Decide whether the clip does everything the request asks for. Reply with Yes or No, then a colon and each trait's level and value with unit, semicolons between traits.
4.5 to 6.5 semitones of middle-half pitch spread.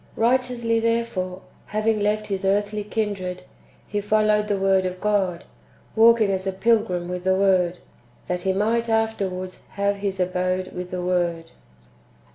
No: average, 2.7 semitones